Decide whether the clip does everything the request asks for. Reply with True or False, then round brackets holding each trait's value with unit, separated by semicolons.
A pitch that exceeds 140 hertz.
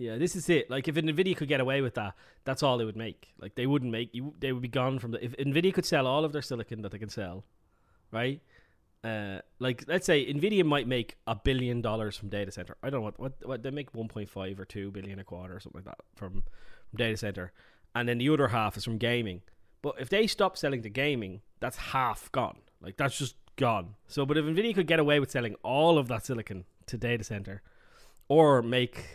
False (120 Hz)